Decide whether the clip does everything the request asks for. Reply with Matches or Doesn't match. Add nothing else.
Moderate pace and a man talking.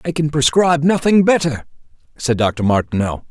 Matches